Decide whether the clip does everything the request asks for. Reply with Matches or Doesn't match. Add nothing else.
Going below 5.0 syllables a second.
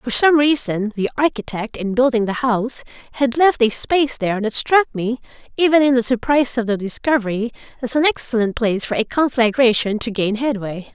Doesn't match